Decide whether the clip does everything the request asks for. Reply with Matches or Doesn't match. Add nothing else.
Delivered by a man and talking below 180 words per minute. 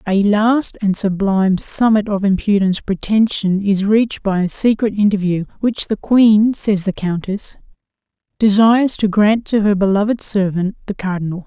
Doesn't match